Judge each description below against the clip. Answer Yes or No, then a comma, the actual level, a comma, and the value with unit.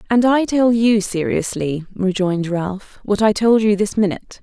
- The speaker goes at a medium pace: Yes, average, 175 wpm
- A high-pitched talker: Yes, high, 205 Hz